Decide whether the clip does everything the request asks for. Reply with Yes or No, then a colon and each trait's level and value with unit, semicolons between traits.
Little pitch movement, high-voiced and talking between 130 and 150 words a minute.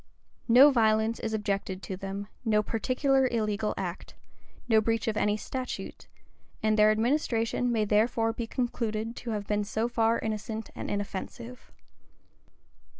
Yes: narrow, 1.8 semitones; high, 220 Hz; average, 140 wpm